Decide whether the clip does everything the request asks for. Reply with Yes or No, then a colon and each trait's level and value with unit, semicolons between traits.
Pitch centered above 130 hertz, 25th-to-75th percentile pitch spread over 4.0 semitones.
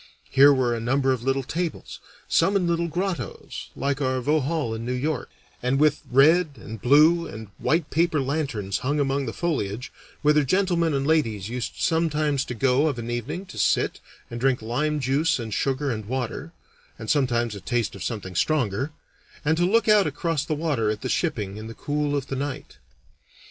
Yes: medium, 140 Hz; average, 4.5 semitones